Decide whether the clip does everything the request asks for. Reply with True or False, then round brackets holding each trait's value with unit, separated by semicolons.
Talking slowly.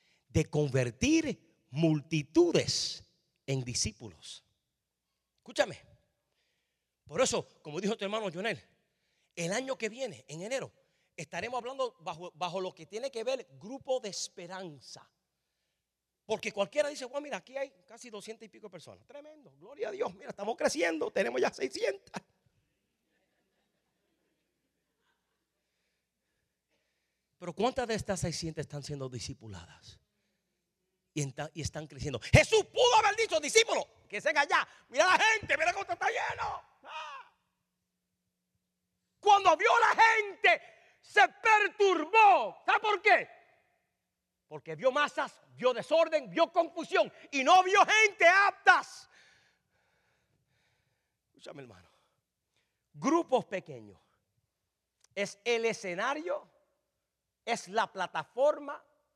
True (115 wpm)